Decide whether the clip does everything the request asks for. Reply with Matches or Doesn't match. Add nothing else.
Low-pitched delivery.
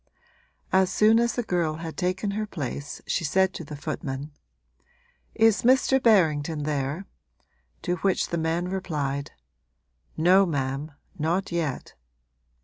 Doesn't match